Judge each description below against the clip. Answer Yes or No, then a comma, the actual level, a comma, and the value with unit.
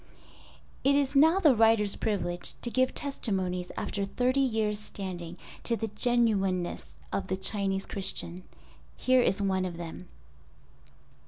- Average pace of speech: No, slow, 130 wpm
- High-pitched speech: Yes, high, 205 Hz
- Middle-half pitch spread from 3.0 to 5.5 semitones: Yes, average, 4.7 semitones